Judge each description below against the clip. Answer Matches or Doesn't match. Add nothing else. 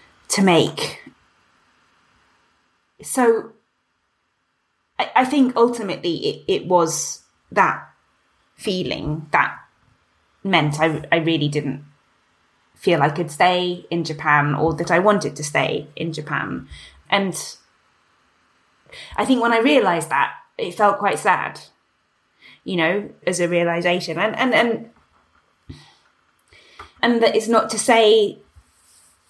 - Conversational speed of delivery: Doesn't match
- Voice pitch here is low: Doesn't match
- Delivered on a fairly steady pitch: Doesn't match